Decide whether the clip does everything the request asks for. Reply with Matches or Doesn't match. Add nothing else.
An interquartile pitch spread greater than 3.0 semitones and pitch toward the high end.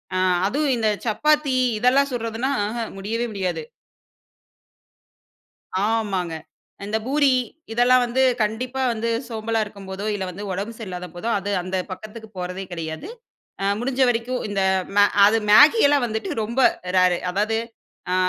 Matches